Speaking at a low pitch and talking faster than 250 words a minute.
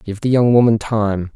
No: low, 110 Hz; fast, 220 wpm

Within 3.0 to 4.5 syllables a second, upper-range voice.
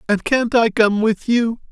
Yes: 4.1 syllables/s; high, 225 Hz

